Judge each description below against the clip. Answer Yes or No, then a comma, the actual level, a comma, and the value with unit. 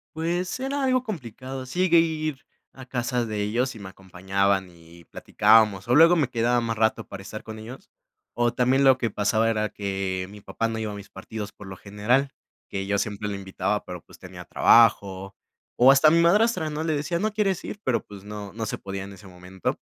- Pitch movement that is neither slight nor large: No, wide, 5.9 semitones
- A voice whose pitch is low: Yes, low, 115 Hz